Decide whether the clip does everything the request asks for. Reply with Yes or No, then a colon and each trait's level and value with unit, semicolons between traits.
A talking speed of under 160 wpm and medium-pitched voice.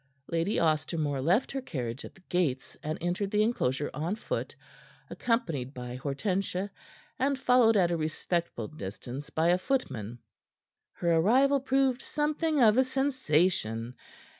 Yes: average, 140 wpm; medium, 175 Hz